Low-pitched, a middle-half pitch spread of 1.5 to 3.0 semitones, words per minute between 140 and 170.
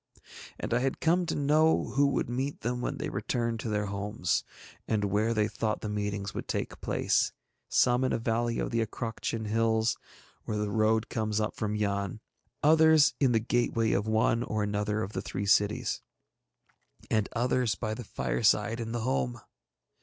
No: low, 110 Hz; narrow, 2.6 semitones; average, 180 wpm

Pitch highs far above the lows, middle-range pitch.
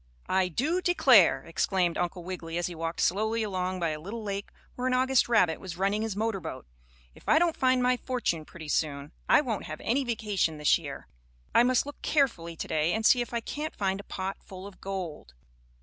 No: wide, 6.1 semitones; high, 195 Hz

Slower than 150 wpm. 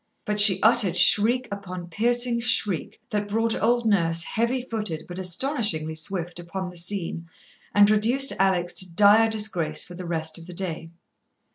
No: average, 160 wpm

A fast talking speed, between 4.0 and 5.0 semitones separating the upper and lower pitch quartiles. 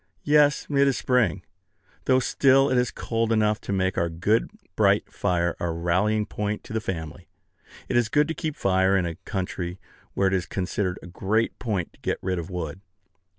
No: average, 195 wpm; average, 4.3 semitones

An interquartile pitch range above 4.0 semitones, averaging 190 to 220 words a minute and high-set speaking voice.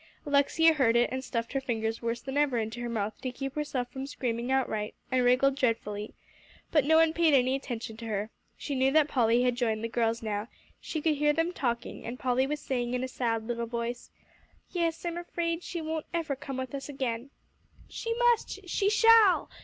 Yes: average, 4.4 semitones; fast, 205 wpm; very high, 260 Hz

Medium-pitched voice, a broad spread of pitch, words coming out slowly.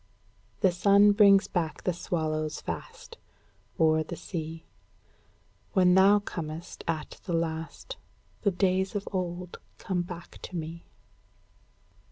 No: medium, 175 Hz; average, 3.0 semitones; slow, 120 wpm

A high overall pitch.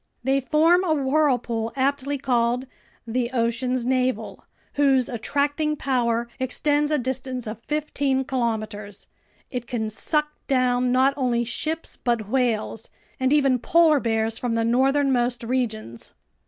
Yes: very high, 255 Hz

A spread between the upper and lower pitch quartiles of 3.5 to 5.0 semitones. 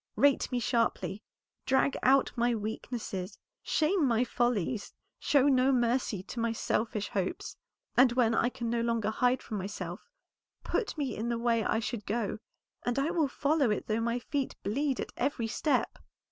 No: average, 3.1 semitones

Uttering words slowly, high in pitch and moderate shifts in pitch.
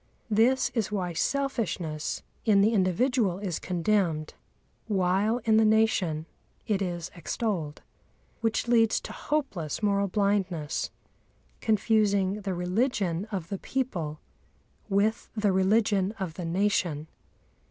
Yes: slow, 115 wpm; high, 200 Hz; average, 3.6 semitones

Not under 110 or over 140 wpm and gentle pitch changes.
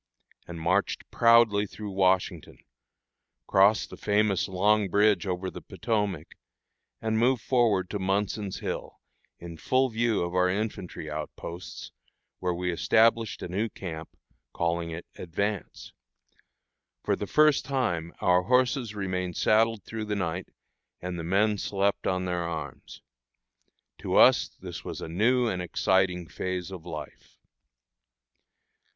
No: slow, 135 wpm; average, 3.4 semitones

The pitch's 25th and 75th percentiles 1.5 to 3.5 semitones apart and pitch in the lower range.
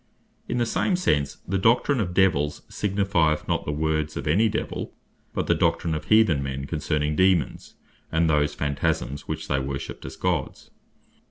No: average, 4.8 semitones; very low, 80 Hz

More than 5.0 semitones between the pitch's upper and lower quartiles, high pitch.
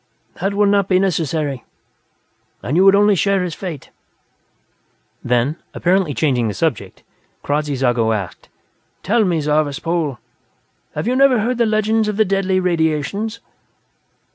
No: wide, 5.6 semitones; medium, 180 Hz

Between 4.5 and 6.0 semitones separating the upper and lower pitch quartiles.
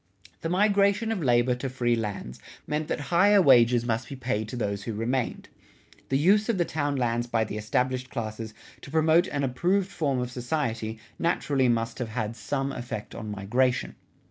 Yes: average, 5.1 semitones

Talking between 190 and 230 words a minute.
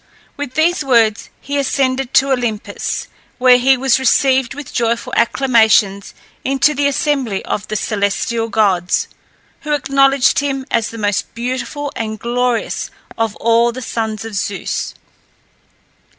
No: slow, 135 wpm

